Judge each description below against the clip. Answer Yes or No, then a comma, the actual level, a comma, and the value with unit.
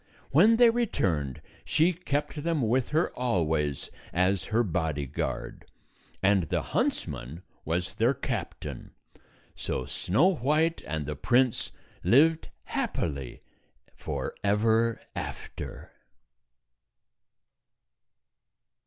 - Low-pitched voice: Yes, low, 110 Hz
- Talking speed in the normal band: No, slow, 90 wpm